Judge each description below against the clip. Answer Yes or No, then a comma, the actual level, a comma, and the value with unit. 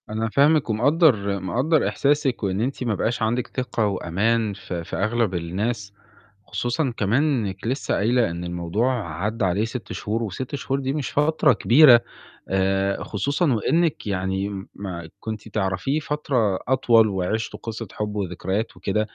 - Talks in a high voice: No, low, 110 Hz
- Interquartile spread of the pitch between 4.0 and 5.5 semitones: Yes, average, 4.8 semitones